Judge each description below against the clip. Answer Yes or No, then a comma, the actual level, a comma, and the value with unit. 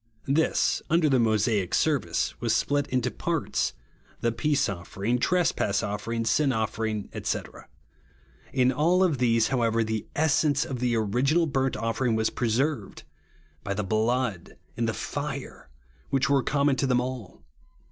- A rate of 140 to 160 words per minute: Yes, average, 150 wpm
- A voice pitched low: Yes, low, 125 Hz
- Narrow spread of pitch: No, average, 4.2 semitones